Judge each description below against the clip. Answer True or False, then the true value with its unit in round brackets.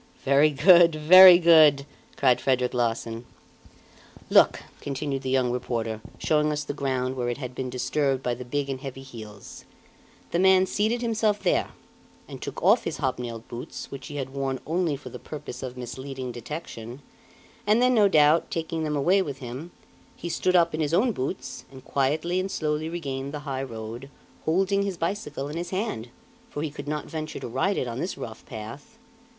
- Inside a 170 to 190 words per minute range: True (185 wpm)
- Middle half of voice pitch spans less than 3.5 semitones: False (4.7 semitones)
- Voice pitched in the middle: True (145 Hz)